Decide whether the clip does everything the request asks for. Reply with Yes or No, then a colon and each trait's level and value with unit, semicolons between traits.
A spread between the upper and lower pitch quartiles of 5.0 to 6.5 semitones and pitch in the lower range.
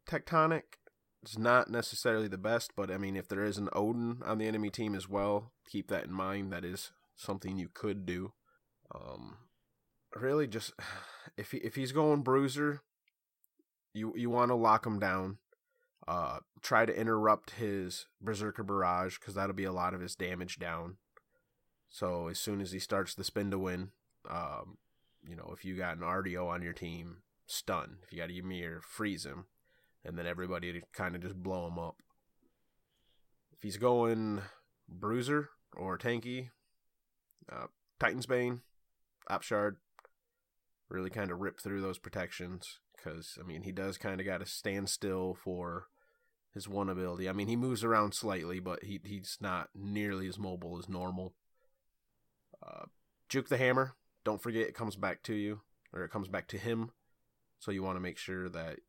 No: average, 3.8 semitones; low, 100 Hz